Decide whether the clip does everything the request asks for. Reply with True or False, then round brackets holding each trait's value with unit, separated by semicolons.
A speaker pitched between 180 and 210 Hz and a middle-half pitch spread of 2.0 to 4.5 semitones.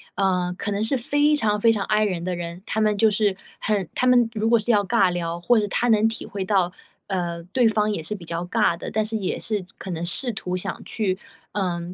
True (205 Hz; 3.5 semitones)